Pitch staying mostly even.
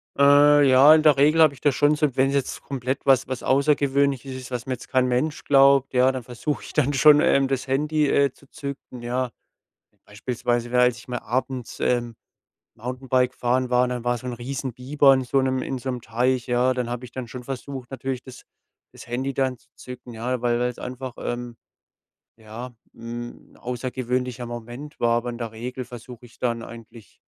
Yes: narrow, 1.9 semitones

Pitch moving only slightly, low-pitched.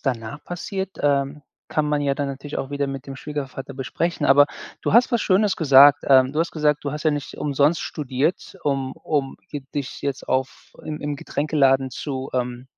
No: narrow, 1.9 semitones; medium, 145 Hz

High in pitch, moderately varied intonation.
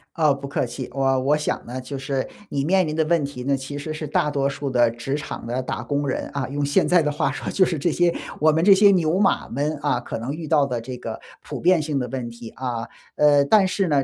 No: medium, 145 Hz; average, 3.0 semitones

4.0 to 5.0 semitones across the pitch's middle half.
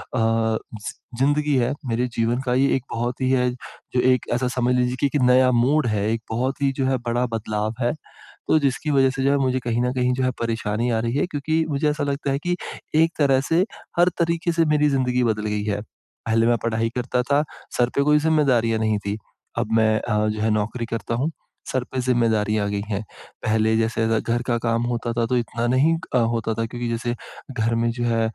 No: average, 2.9 semitones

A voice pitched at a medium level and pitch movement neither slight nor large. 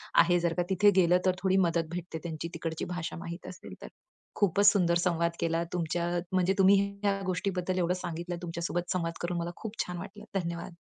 No: medium, 175 Hz; narrow, 1.7 semitones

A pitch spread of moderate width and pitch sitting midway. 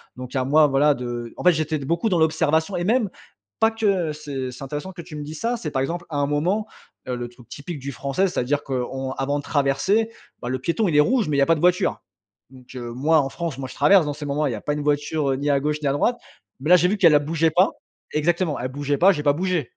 Yes: average, 4.1 semitones; medium, 150 Hz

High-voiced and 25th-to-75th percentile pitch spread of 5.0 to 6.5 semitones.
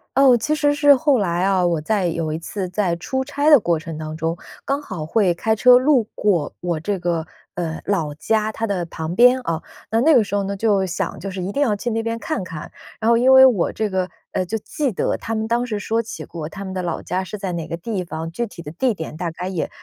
Yes: high, 195 Hz; average, 5.3 semitones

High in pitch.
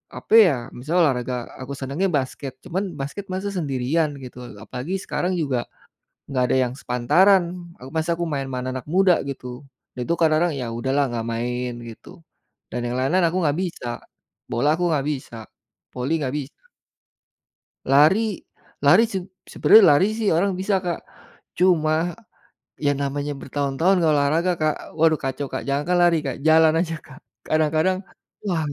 No: medium, 150 Hz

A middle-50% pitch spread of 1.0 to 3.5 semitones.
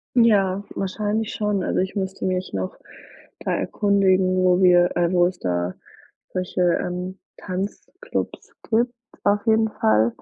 Yes: narrow, 2.5 semitones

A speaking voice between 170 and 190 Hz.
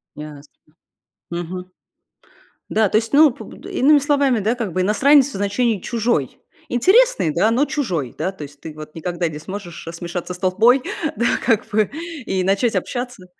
No: high, 205 Hz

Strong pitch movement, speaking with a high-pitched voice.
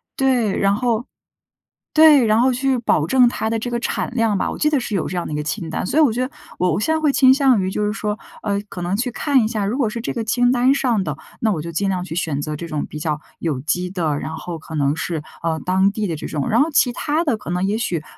Yes: wide, 6.5 semitones; high, 210 Hz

